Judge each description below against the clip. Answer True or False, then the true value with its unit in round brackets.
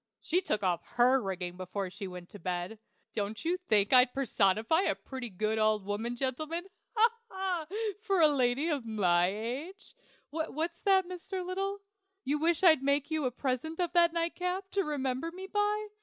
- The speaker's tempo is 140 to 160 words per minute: False (175 wpm)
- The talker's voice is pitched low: False (275 Hz)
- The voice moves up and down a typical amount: False (8.4 semitones)